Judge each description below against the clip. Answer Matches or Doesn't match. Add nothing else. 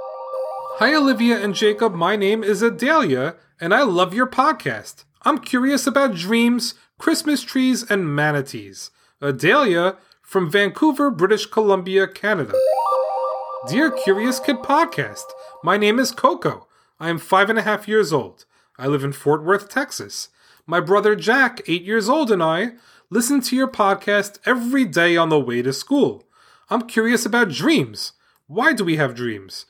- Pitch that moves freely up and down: Matches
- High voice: Matches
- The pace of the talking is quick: Doesn't match